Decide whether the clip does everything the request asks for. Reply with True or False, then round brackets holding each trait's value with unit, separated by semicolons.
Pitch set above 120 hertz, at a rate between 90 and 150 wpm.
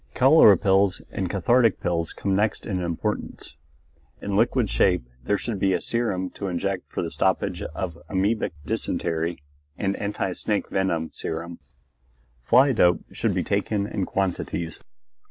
False (95 Hz; 140 wpm)